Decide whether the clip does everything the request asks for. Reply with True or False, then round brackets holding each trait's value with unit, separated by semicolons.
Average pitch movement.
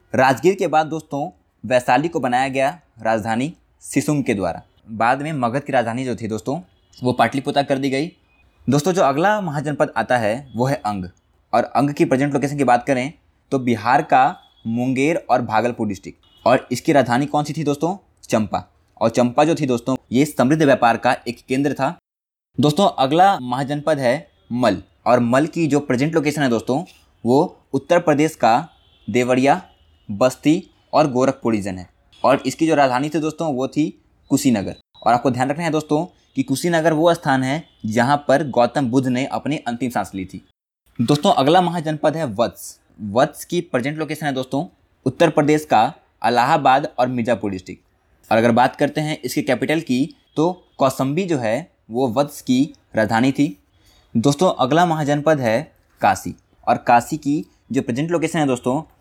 True (3.8 semitones)